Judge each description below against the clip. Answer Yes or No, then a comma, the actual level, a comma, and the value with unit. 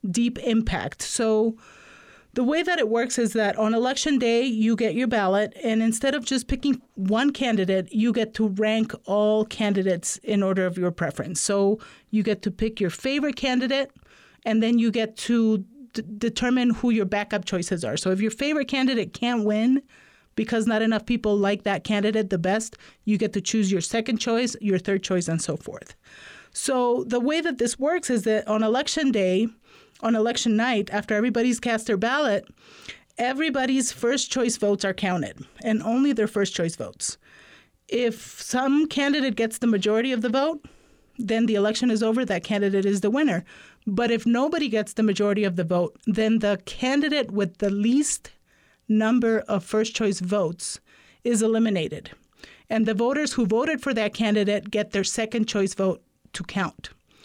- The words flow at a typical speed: Yes, average, 180 wpm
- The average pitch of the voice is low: No, high, 225 Hz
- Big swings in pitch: No, average, 2.9 semitones